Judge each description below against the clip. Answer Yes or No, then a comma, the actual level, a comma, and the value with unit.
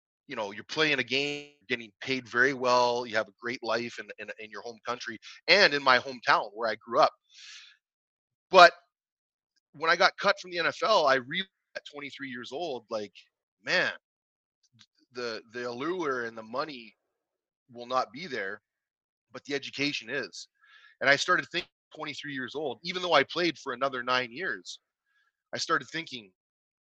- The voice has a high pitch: No, low, 135 Hz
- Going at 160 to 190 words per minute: Yes, average, 170 wpm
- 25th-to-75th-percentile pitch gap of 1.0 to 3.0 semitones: No, average, 4.5 semitones